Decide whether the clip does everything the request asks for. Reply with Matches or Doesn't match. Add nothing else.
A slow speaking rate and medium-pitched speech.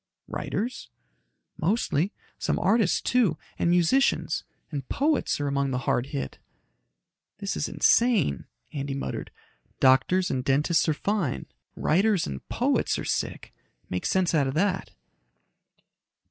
Matches